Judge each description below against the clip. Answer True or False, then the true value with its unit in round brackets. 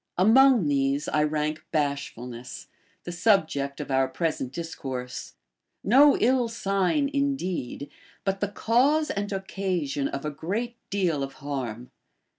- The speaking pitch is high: False (170 Hz)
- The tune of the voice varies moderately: False (7.5 semitones)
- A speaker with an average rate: False (130 wpm)